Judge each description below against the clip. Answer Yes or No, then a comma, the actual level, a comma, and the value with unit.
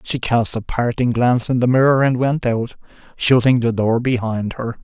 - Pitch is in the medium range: No, low, 120 Hz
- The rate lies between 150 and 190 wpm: No, average, 200 wpm